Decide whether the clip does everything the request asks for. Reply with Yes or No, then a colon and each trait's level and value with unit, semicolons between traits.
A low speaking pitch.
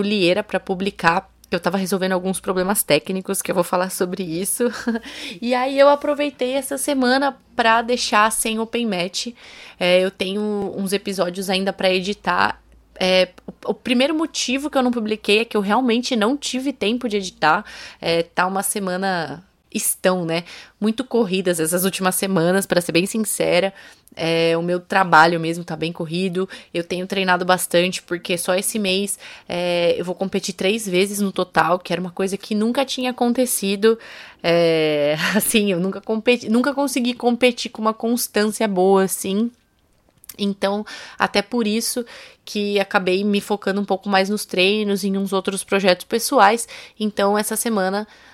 No: high, 200 Hz